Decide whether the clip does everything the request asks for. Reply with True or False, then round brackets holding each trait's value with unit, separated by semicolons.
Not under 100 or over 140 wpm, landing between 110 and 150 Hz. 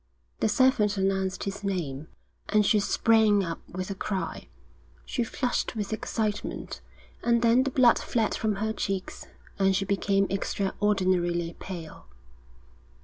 False (135 wpm; 200 Hz)